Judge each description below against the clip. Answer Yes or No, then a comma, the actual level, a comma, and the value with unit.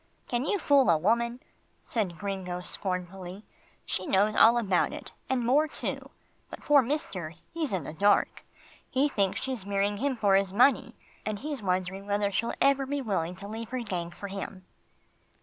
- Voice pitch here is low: No, high, 205 Hz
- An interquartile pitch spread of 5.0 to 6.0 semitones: Yes, average, 5.3 semitones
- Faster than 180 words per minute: No, average, 175 wpm